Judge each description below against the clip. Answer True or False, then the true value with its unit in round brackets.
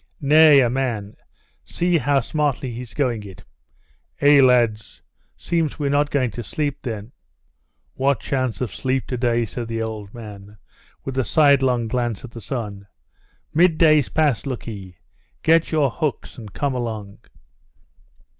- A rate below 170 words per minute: True (145 wpm)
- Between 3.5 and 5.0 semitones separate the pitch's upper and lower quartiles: True (4.2 semitones)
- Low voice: True (125 Hz)